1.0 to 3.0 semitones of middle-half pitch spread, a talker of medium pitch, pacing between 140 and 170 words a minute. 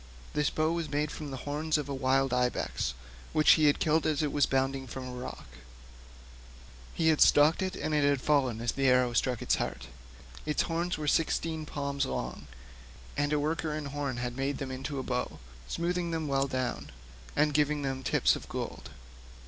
No: narrow, 2.5 semitones; medium, 145 Hz; average, 200 wpm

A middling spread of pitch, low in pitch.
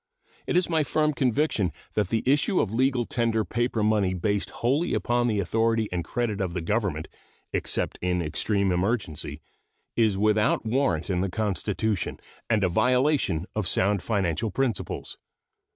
Yes: average, 4.4 semitones; low, 110 Hz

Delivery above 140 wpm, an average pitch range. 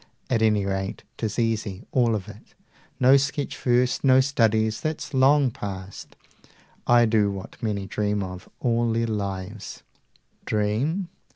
No: slow, 135 wpm; average, 3.5 semitones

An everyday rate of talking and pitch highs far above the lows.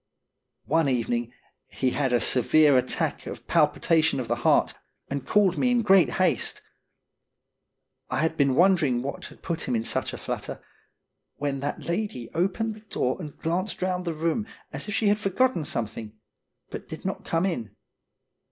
Yes: average, 170 wpm; wide, 6.6 semitones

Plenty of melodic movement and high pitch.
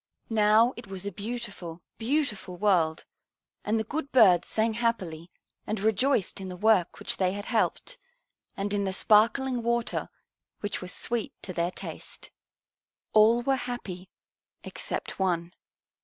No: average, 4.1 semitones; high, 210 Hz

